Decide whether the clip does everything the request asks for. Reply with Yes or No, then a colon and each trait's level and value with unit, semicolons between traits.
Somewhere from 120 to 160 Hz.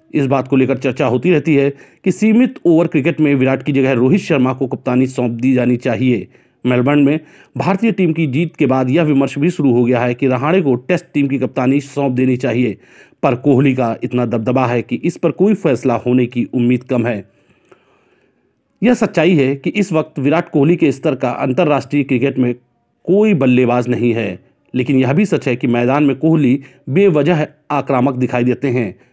Yes: low, 135 Hz